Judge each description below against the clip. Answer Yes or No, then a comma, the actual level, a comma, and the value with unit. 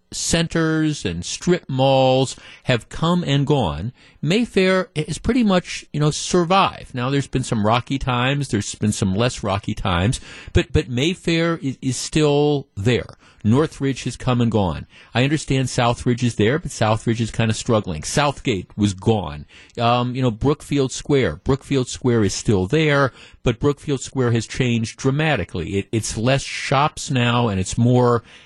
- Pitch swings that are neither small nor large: Yes, average, 4.4 semitones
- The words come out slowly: No, average, 160 wpm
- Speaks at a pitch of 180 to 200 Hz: No, low, 125 Hz